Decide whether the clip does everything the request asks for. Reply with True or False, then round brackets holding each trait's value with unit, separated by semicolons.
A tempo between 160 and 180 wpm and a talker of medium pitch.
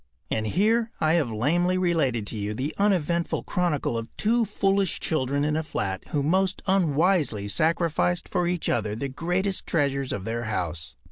True (165 wpm; 155 Hz)